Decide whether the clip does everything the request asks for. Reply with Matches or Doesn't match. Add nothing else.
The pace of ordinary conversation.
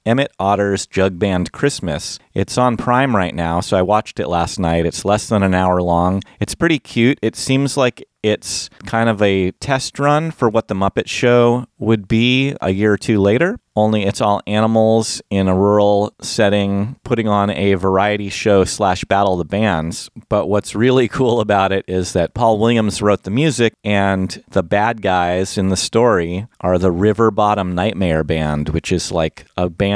Matches